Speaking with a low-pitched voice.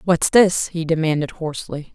No: medium, 165 Hz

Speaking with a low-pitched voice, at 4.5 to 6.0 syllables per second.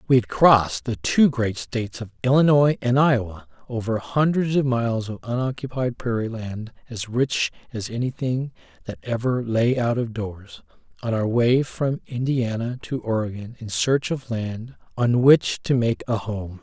Yes: low, 120 Hz; 4.6 syllables/s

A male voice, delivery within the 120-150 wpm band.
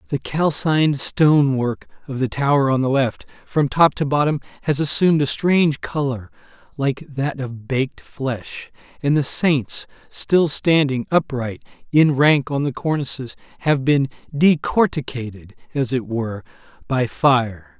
Yes: male; average, 145 wpm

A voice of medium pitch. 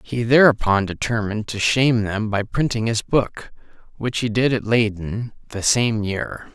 No: low, 110 Hz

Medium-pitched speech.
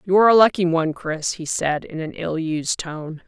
Yes: medium, 170 Hz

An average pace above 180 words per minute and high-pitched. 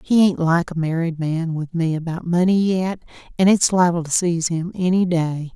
No: fast, 205 wpm; medium, 170 Hz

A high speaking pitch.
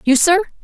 Yes: very high, 330 Hz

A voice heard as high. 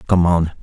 No: very low, 85 Hz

